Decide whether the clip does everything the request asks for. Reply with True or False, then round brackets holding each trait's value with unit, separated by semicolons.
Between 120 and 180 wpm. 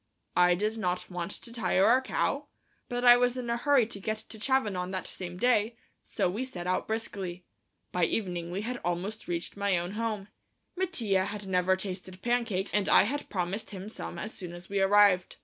False (200 wpm)